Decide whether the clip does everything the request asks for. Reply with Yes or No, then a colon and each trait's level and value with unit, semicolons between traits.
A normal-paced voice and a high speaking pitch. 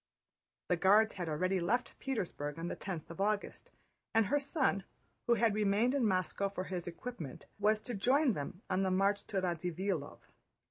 Yes: average, 175 wpm; high, 195 Hz